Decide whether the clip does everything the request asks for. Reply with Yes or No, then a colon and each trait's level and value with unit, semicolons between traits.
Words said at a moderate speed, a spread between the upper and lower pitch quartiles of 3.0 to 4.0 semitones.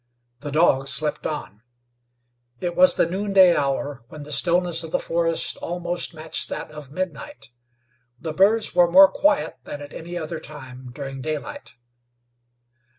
Yes: average, 150 wpm; average, 3.6 semitones